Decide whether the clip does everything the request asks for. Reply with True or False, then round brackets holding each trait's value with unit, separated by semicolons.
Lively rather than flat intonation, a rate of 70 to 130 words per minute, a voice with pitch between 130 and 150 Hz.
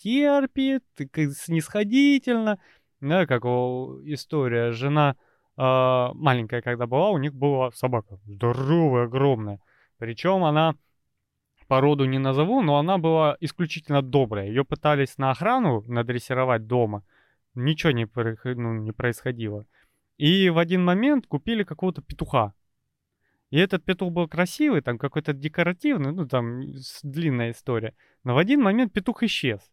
True (5.8 semitones; 125 wpm; 140 Hz)